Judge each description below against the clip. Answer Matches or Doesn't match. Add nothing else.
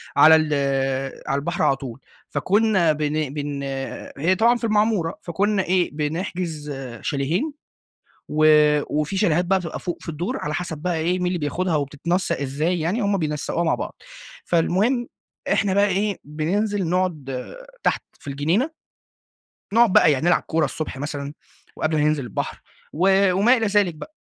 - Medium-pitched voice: Matches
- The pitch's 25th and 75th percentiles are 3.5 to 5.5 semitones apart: Matches